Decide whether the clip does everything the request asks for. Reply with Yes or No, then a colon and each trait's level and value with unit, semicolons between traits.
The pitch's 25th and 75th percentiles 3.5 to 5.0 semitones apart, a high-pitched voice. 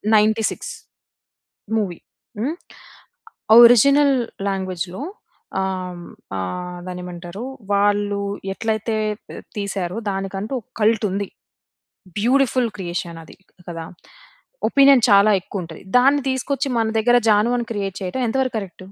Yes: average, 4.5 semitones; high, 205 Hz